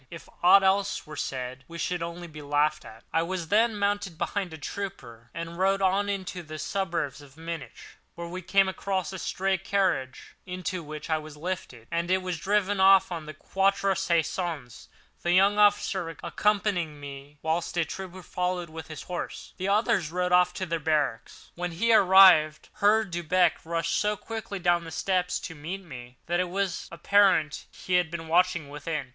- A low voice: No, medium, 175 Hz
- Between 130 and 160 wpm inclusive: No, average, 185 wpm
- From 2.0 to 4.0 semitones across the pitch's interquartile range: Yes, average, 3.4 semitones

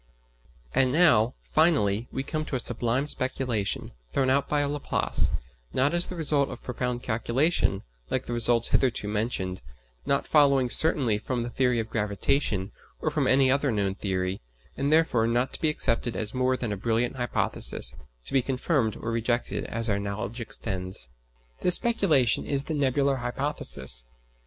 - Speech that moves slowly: No, average, 160 wpm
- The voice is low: Yes, low, 125 Hz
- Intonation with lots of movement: No, average, 4.0 semitones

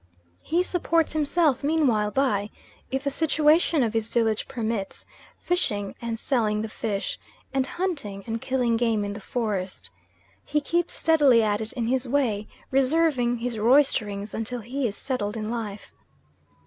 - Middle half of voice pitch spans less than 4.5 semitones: No, average, 4.8 semitones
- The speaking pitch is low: No, high, 240 Hz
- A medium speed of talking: Yes, average, 150 wpm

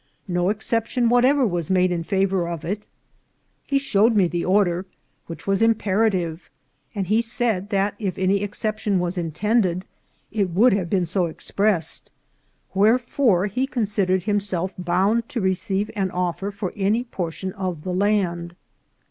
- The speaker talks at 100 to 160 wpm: Yes, average, 150 wpm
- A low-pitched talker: No, high, 195 Hz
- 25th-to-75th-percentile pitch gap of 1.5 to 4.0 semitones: Yes, average, 3.1 semitones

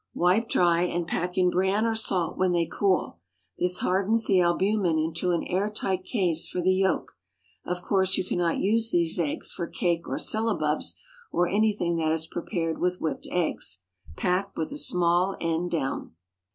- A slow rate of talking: No, average, 175 wpm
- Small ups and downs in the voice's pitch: Yes, narrow, 2.3 semitones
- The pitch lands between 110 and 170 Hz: No, medium, 180 Hz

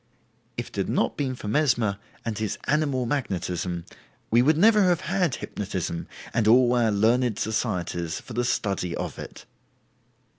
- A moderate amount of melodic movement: No, wide, 5.7 semitones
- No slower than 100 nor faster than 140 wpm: No, average, 155 wpm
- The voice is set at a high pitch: No, low, 115 Hz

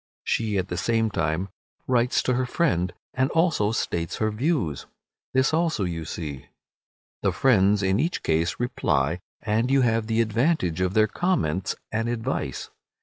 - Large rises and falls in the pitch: Yes, wide, 6.1 semitones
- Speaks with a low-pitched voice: Yes, low, 110 Hz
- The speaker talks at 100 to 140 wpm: No, average, 155 wpm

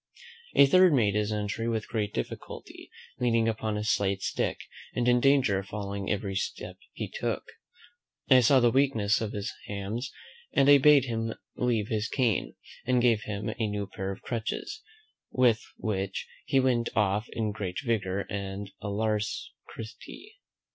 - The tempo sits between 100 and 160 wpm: Yes, average, 155 wpm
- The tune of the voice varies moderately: Yes, average, 3.2 semitones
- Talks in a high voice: No, low, 110 Hz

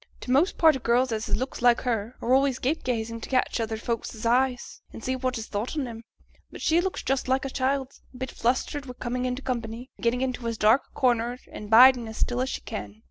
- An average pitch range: No, narrow, 2.2 semitones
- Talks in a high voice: Yes, very high, 250 Hz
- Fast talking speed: Yes, fast, 245 wpm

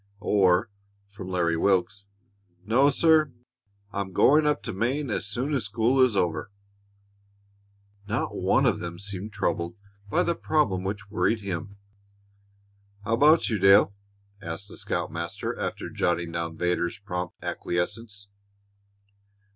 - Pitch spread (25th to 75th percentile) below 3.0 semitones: No, average, 4.4 semitones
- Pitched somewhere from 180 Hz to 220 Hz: No, low, 100 Hz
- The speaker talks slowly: Yes, slow, 130 wpm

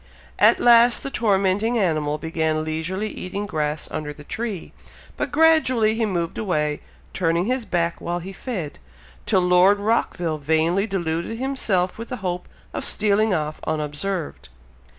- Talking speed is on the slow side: No, average, 145 wpm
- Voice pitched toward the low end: No, medium, 185 Hz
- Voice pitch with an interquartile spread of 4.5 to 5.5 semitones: Yes, average, 5.2 semitones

